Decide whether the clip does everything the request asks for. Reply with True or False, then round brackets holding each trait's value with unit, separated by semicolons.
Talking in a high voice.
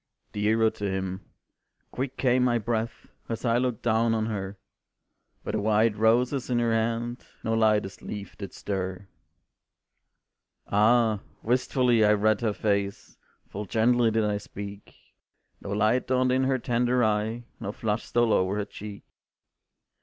False (110 Hz)